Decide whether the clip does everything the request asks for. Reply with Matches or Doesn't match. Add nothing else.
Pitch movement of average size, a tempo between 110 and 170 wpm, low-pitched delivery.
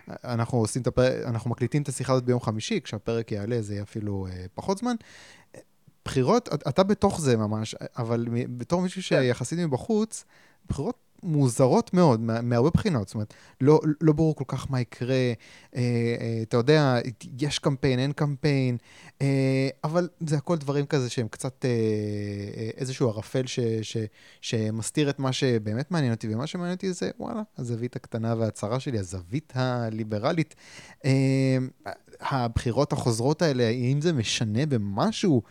Matches